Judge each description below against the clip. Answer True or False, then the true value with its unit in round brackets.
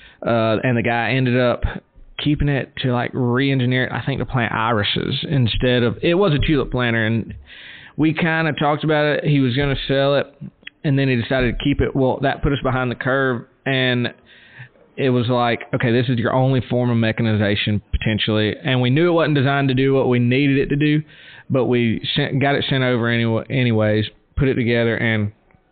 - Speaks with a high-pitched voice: False (125 Hz)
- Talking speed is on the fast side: True (210 wpm)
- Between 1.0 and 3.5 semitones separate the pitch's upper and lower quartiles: True (2.9 semitones)